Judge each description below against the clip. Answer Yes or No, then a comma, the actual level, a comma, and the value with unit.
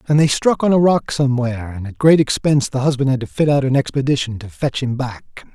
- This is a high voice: No, low, 135 Hz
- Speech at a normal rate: No, fast, 250 wpm